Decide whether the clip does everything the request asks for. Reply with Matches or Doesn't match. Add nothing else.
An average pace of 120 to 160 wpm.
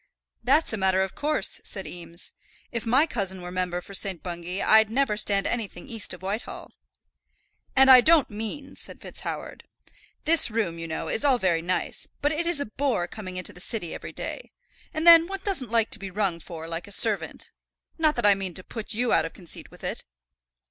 Doesn't match